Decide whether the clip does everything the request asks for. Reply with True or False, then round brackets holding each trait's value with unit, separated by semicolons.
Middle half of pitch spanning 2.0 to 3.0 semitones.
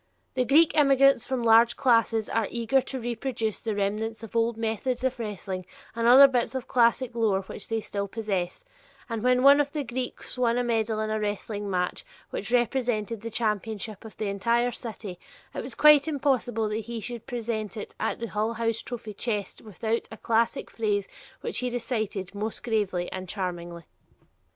True (2.6 semitones)